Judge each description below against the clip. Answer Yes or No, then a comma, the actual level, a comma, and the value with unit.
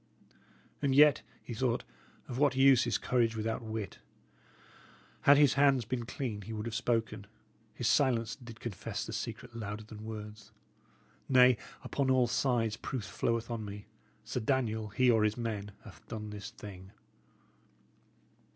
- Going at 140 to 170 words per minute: Yes, average, 150 wpm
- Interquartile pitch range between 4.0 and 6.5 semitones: No, average, 3.0 semitones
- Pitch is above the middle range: No, low, 115 Hz